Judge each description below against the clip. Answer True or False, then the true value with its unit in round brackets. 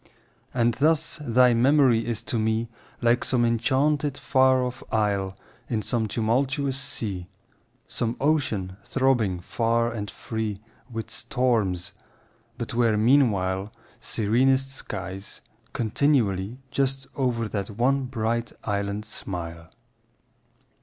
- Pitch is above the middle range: False (115 Hz)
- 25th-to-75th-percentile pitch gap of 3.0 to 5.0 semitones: True (3.8 semitones)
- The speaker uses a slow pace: True (105 wpm)